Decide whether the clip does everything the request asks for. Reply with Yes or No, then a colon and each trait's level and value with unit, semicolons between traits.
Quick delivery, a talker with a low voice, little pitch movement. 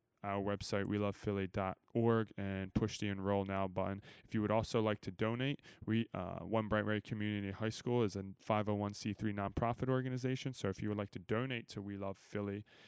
No: average, 190 wpm; low, 105 Hz; narrow, 2.3 semitones